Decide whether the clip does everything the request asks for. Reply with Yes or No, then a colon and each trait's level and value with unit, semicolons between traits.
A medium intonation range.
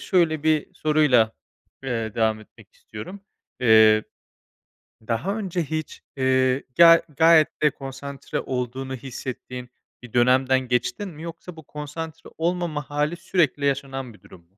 Yes: average, 4.2 semitones